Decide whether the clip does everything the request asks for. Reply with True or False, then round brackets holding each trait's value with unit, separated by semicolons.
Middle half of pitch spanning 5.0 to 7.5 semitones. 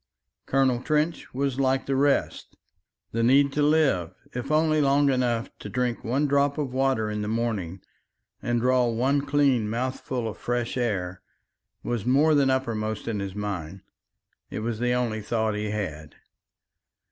False (4.1 semitones)